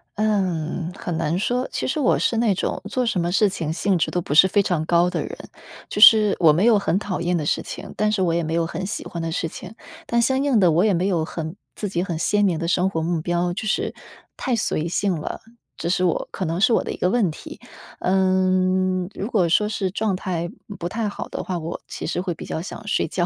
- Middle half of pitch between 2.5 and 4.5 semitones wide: Yes, average, 3.4 semitones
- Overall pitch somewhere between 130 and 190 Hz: Yes, medium, 185 Hz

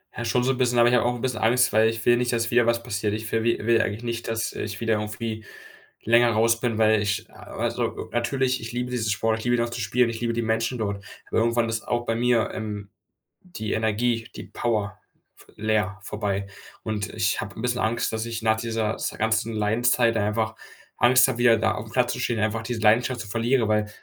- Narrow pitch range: Yes, narrow, 1.7 semitones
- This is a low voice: Yes, low, 115 Hz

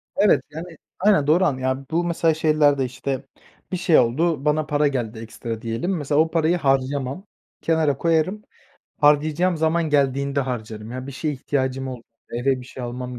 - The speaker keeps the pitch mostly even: No, average, 3.7 semitones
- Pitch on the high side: No, medium, 145 Hz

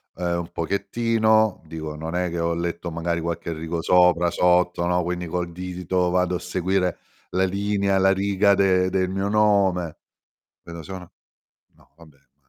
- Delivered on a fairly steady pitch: Yes, narrow, 2.1 semitones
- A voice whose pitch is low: Yes, very low, 90 Hz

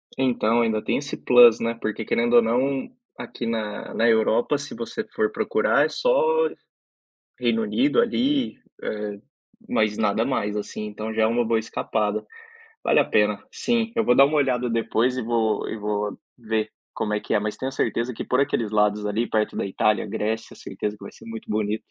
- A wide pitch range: No, average, 3.4 semitones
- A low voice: Yes, low, 115 Hz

